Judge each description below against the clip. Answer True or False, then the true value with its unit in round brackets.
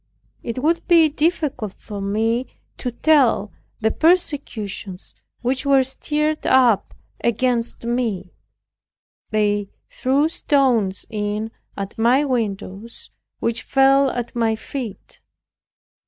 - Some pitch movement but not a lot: True (4.4 semitones)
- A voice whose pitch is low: False (240 Hz)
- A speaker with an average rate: False (105 wpm)